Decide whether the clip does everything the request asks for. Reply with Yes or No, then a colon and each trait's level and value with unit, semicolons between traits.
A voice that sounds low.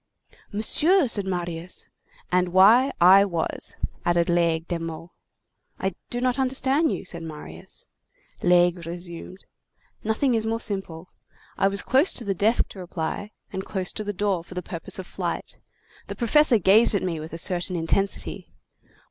No: high, 190 Hz